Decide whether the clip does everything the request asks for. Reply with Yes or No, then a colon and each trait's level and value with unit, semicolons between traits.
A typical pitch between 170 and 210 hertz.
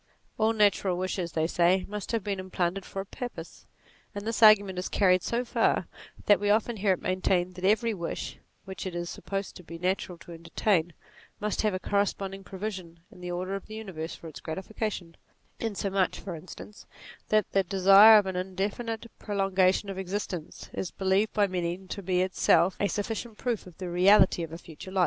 Yes: high, 190 Hz